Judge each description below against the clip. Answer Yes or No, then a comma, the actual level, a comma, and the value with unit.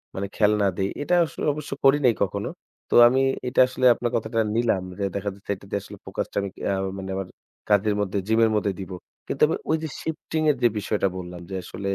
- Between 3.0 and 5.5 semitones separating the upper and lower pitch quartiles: Yes, average, 4.1 semitones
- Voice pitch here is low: Yes, low, 105 Hz